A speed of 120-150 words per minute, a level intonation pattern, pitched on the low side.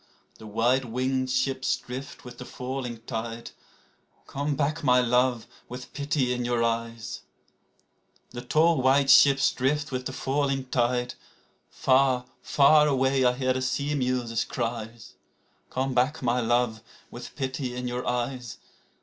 Yes: average, 140 wpm; narrow, 1.8 semitones; low, 125 Hz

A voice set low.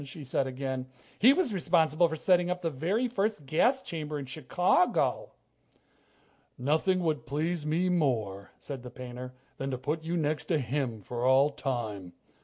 No: medium, 150 Hz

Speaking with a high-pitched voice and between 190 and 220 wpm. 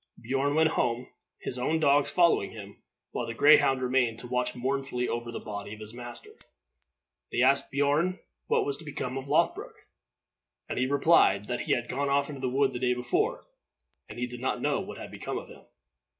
No: low, 130 Hz; average, 195 wpm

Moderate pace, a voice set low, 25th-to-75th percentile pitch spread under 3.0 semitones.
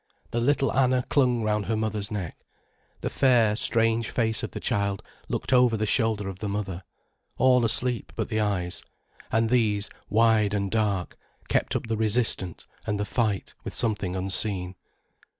Yes: average, 165 wpm; low, 110 Hz; narrow, 2.5 semitones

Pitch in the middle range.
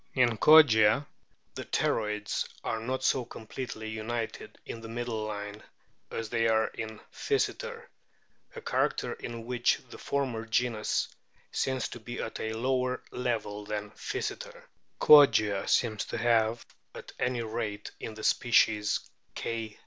No: low, 115 Hz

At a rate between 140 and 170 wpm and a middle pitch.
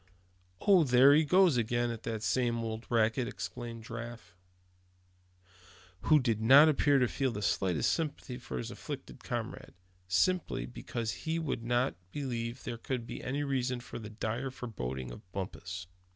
No: average, 155 wpm; low, 120 Hz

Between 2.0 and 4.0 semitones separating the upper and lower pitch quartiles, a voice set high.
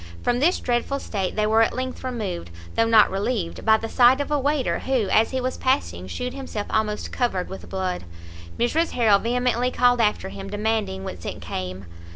No: average, 4.4 semitones; high, 225 Hz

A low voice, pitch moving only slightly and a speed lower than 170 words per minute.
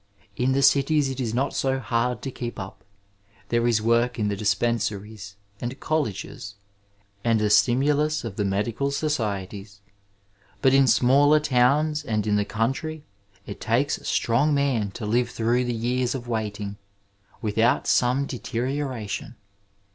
No: low, 120 Hz; average, 4.0 semitones; average, 150 wpm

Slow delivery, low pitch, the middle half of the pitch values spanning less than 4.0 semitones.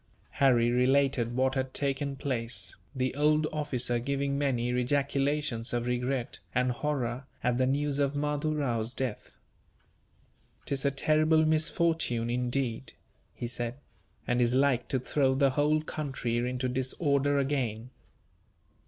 Yes: slow, 130 wpm; low, 130 Hz; average, 2.8 semitones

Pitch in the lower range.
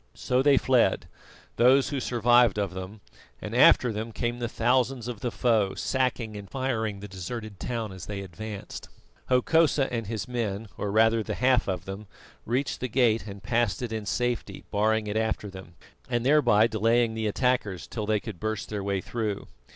Yes: low, 110 Hz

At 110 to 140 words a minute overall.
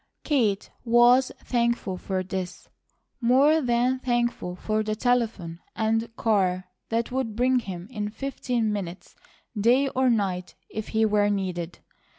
Yes: slow, 135 wpm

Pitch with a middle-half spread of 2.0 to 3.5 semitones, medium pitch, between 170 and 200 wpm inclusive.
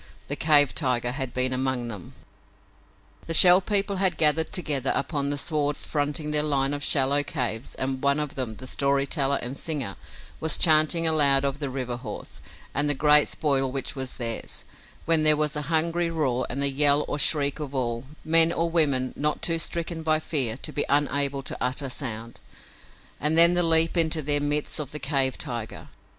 Yes: average, 2.9 semitones; medium, 145 Hz; average, 190 wpm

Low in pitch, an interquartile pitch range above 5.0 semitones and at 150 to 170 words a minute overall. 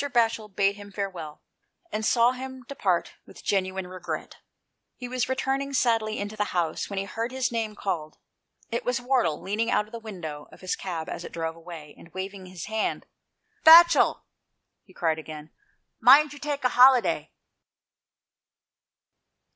No: high, 210 Hz; wide, 5.4 semitones; average, 160 wpm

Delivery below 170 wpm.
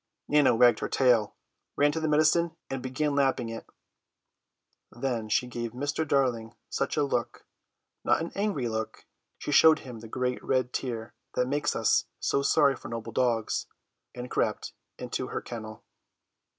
Yes: average, 160 wpm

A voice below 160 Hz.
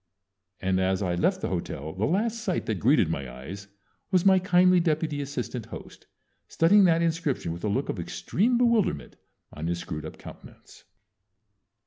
Yes: medium, 140 Hz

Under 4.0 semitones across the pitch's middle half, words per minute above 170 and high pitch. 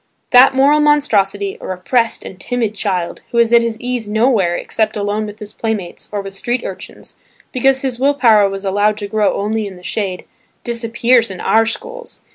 Yes: average, 3.4 semitones; average, 190 wpm; high, 220 Hz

